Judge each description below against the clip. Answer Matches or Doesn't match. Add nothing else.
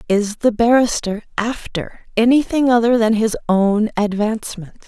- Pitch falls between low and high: Doesn't match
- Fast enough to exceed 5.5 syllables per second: Doesn't match